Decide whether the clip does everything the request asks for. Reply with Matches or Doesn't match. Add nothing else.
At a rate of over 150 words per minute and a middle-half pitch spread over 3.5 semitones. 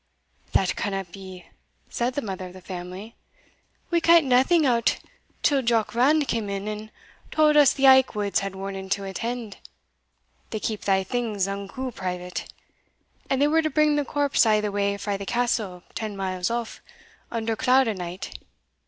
Matches